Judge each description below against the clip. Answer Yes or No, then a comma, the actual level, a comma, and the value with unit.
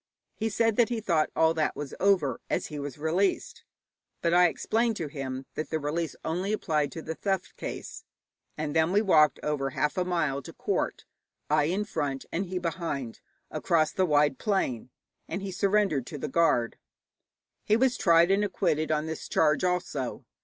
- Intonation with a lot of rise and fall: No, average, 4.4 semitones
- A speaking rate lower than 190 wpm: Yes, average, 180 wpm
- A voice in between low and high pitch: Yes, medium, 165 Hz